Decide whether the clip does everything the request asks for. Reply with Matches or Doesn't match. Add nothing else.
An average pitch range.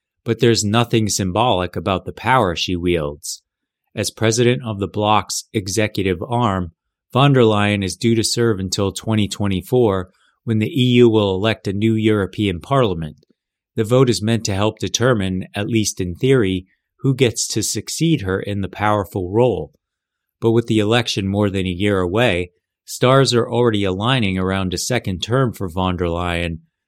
Matches